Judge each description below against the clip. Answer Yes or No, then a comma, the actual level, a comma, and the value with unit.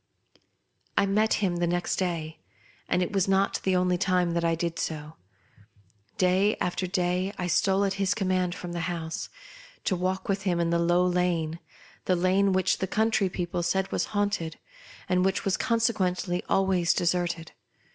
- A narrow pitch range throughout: Yes, narrow, 1.9 semitones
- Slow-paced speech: No, average, 175 wpm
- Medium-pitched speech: Yes, medium, 180 Hz